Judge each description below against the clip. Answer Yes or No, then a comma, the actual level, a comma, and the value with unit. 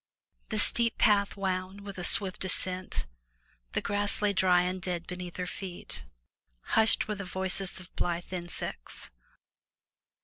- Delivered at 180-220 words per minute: No, average, 140 wpm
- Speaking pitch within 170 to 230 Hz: Yes, medium, 185 Hz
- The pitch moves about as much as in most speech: No, narrow, 2.0 semitones